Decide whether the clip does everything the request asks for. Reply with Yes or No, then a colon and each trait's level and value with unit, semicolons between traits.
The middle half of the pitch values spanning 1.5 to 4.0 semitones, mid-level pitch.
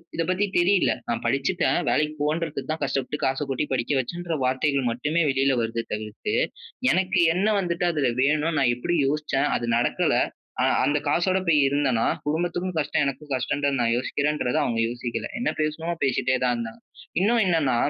No: average, 4.7 semitones; medium, 145 Hz